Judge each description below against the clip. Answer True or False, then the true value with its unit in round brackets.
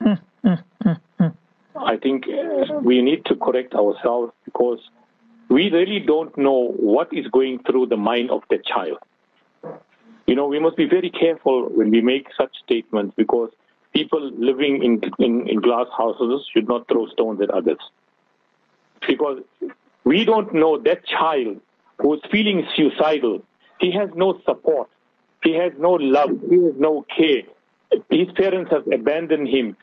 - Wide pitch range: True (7.7 semitones)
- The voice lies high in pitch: False (165 Hz)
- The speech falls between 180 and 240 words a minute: False (150 wpm)